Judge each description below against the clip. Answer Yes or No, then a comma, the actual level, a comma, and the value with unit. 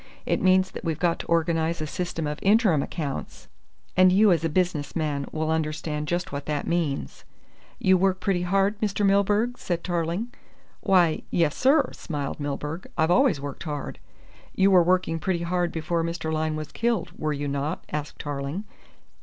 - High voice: No, medium, 170 Hz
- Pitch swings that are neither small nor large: Yes, average, 3.5 semitones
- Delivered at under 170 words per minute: No, average, 175 wpm